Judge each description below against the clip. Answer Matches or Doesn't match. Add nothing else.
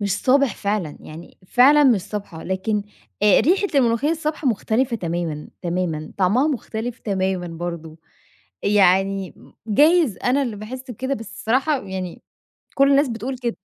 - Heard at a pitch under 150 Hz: Doesn't match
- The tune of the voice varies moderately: Doesn't match